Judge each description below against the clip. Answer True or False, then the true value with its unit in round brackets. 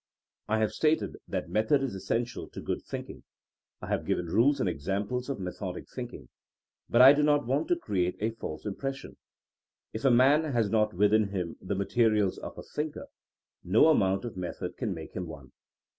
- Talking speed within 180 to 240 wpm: True (185 wpm)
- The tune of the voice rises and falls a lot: True (5.7 semitones)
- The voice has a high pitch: False (110 Hz)